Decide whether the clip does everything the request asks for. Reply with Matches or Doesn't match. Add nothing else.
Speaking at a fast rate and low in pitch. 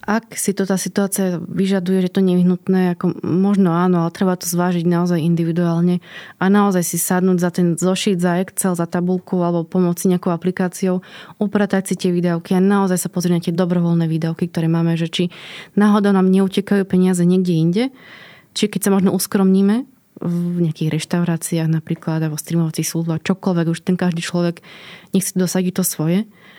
Doesn't match